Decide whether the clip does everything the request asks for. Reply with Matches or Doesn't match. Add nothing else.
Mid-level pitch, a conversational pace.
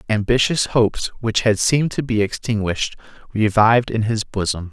Doesn't match